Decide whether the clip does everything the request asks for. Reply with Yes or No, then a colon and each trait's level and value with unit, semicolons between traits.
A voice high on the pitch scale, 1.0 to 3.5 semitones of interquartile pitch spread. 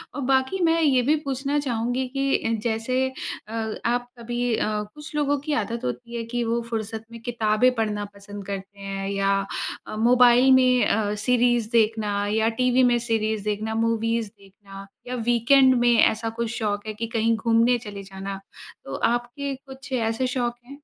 Yes: high, 230 Hz; average, 2.7 semitones